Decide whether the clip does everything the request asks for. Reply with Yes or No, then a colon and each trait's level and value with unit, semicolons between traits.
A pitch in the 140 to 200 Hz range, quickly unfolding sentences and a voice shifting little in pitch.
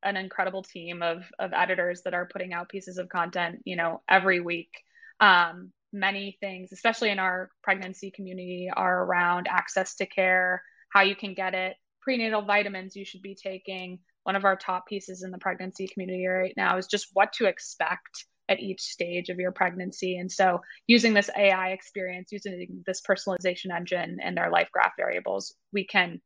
No: medium, 185 Hz; average, 185 wpm; narrow, 1.3 semitones